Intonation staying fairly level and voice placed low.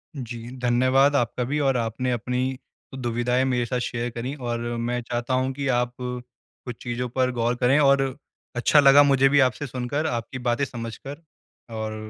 Yes: narrow, 2.0 semitones; low, 125 Hz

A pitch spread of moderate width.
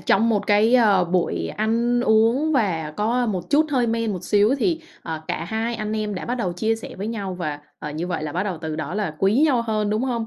Yes: average, 4.4 semitones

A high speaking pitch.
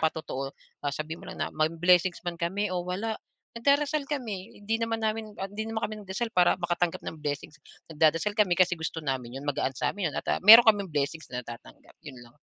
No: medium, 175 Hz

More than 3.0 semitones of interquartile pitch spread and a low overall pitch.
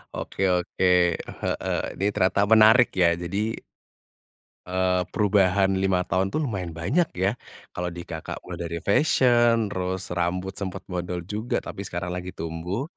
No: narrow, 2.4 semitones; very low, 95 Hz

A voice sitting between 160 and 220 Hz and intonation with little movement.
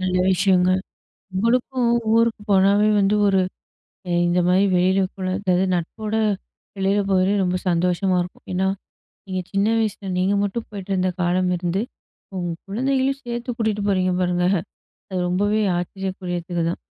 Yes: high, 190 Hz; narrow, 2.3 semitones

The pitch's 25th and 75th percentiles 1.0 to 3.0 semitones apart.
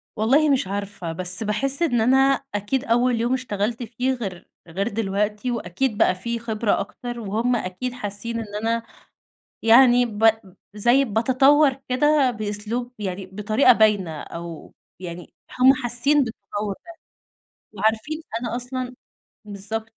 No: average, 3.5 semitones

